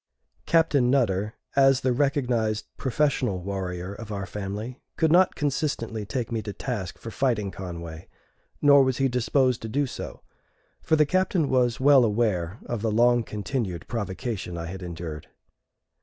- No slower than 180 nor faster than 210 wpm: No, average, 155 wpm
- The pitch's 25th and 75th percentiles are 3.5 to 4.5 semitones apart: No, wide, 5.4 semitones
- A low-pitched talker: Yes, low, 115 Hz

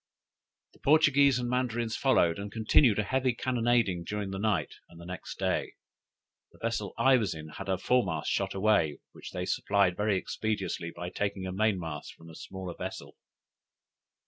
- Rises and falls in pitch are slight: No, average, 4.6 semitones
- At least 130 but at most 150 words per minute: No, average, 170 wpm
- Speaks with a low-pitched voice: Yes, low, 105 Hz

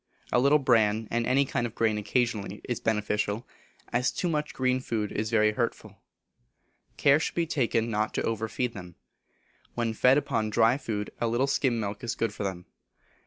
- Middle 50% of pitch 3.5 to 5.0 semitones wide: No, average, 3.0 semitones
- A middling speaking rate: Yes, average, 185 wpm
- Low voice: Yes, low, 115 Hz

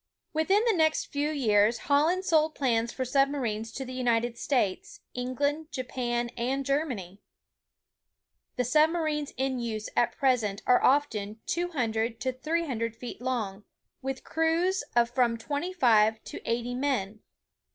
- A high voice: Yes, very high, 255 Hz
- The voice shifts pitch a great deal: No, average, 4.2 semitones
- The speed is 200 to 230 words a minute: No, average, 140 wpm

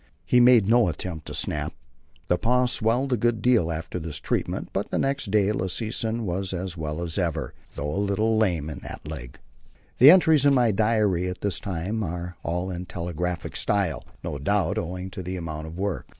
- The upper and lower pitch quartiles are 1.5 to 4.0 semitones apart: No, average, 4.5 semitones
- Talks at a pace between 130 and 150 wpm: No, average, 195 wpm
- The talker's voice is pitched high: No, very low, 95 Hz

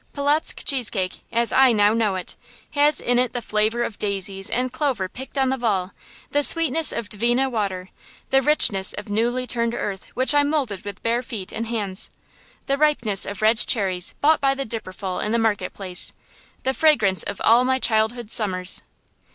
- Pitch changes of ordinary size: Yes, average, 4.6 semitones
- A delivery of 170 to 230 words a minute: Yes, average, 185 wpm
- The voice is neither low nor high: No, high, 230 Hz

